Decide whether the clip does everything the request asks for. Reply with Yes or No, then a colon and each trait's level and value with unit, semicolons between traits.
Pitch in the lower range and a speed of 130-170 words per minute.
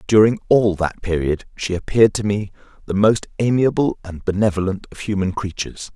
Yes: low, 100 Hz; average, 160 wpm